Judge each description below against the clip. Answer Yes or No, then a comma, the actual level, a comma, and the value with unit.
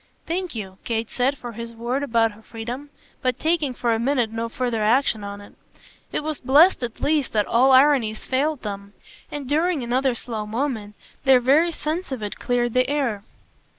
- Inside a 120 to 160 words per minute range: No, average, 185 wpm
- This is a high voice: Yes, high, 245 Hz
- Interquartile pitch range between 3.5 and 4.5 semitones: Yes, average, 4.1 semitones